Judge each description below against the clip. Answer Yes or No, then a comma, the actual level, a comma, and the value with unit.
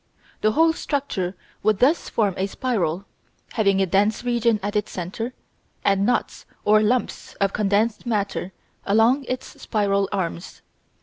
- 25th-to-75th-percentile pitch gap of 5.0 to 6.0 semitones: No, average, 3.3 semitones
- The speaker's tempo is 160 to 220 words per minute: No, average, 140 wpm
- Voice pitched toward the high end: Yes, high, 210 Hz